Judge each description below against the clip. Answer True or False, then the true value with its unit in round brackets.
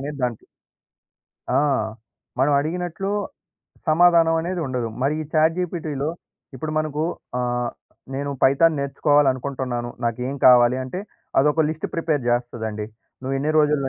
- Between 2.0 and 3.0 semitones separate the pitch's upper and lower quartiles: False (3.8 semitones)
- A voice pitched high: False (140 Hz)